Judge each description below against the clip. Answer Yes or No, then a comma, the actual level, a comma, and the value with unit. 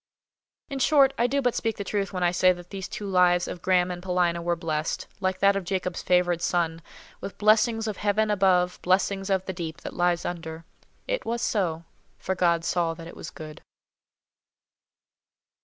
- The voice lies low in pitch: No, medium, 180 Hz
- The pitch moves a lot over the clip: No, average, 2.7 semitones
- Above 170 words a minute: Yes, average, 190 wpm